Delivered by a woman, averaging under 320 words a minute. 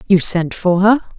Yes: female; average, 200 wpm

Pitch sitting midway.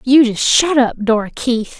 No: high, 245 Hz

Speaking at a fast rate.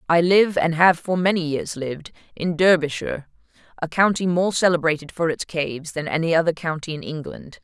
No: average, 180 wpm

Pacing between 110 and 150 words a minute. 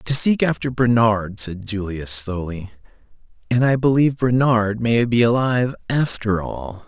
Yes: average, 140 wpm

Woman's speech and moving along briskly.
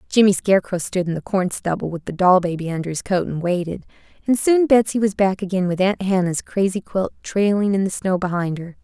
Yes: female; fast, 225 wpm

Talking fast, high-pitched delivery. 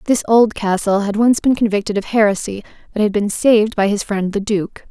Yes: fast, 210 wpm; high, 210 Hz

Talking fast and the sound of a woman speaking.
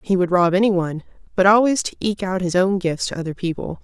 Yes: fast, 235 wpm; female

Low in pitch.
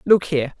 No: medium, 160 Hz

